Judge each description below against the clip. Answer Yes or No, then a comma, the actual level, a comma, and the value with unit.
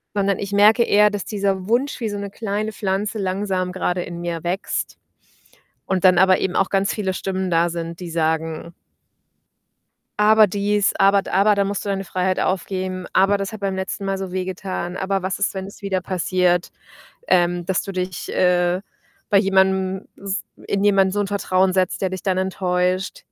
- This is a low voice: No, high, 190 Hz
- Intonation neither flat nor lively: No, narrow, 1.5 semitones